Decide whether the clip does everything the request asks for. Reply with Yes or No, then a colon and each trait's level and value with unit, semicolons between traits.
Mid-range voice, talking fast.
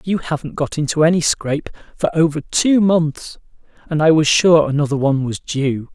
No: medium, 155 Hz; average, 180 wpm